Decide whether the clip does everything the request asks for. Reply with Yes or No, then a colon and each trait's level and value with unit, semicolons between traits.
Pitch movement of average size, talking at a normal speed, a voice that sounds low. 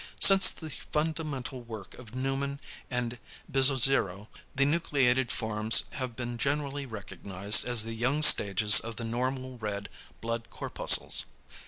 No: average, 3.6 semitones; slow, 130 wpm; low, 125 Hz